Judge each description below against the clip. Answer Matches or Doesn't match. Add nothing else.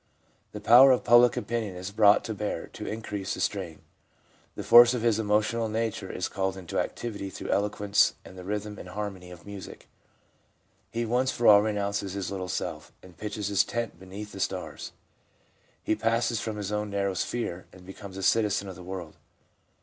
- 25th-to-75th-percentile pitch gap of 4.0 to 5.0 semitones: Doesn't match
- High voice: Doesn't match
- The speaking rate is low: Doesn't match